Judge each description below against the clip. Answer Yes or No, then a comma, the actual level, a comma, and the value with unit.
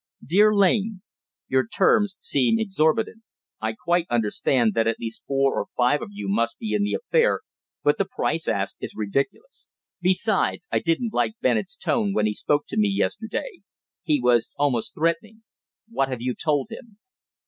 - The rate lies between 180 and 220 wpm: No, average, 170 wpm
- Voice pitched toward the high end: No, medium, 165 Hz